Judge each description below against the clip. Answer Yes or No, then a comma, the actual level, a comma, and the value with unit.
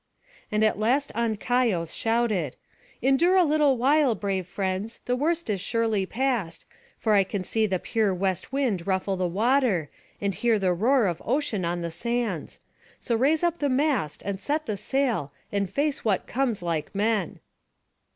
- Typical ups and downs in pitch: No, wide, 5.8 semitones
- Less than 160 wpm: No, average, 170 wpm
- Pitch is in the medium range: No, high, 220 Hz